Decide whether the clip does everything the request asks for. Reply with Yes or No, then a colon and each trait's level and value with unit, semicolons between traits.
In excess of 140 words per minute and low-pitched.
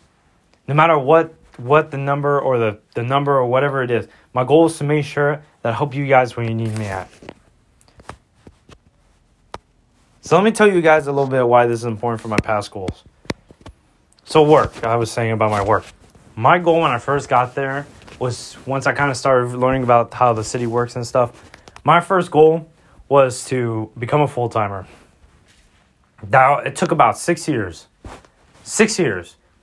Yes: average, 185 wpm; low, 125 Hz